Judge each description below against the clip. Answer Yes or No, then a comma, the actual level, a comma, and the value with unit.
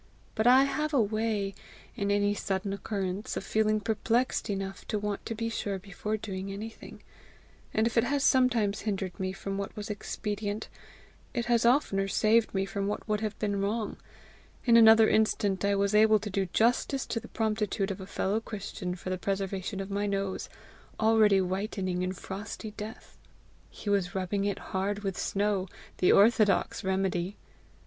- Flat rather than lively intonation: Yes, narrow, 2.0 semitones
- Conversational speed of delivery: Yes, average, 170 wpm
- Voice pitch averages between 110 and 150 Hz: No, high, 205 Hz